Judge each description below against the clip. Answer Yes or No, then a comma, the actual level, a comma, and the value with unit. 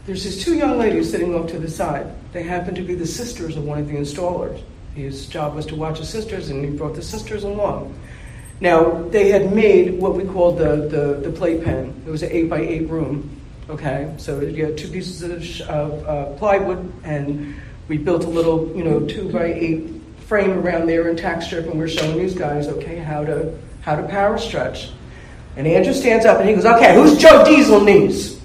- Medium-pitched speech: Yes, medium, 165 Hz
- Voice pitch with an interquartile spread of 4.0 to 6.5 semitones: No, average, 3.6 semitones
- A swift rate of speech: Yes, fast, 215 wpm